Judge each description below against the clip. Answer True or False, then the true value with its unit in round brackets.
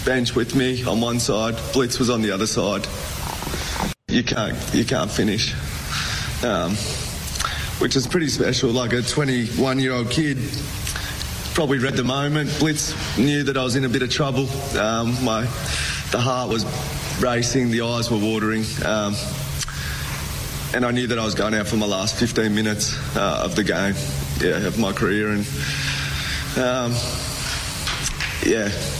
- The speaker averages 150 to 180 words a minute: True (155 wpm)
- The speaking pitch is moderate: False (120 Hz)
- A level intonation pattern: False (3.5 semitones)